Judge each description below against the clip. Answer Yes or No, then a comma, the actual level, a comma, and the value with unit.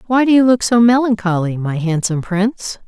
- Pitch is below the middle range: No, high, 210 Hz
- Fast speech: No, average, 190 wpm